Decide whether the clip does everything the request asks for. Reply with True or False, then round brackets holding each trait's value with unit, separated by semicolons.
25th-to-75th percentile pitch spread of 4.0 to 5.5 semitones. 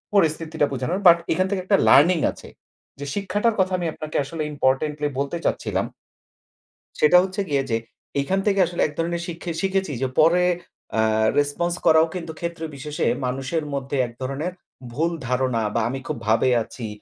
True (4.3 semitones)